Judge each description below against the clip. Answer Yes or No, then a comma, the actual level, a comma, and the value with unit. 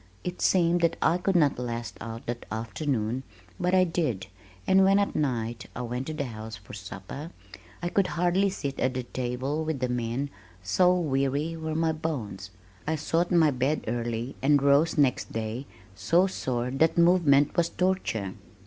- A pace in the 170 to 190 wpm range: Yes, average, 175 wpm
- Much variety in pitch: Yes, wide, 5.8 semitones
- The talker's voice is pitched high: No, medium, 140 Hz